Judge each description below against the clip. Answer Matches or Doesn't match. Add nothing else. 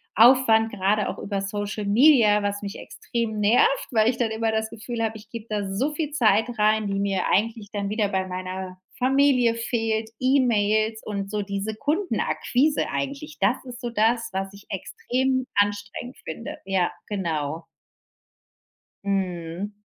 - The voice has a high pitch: Matches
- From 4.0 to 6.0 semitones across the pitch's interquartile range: Doesn't match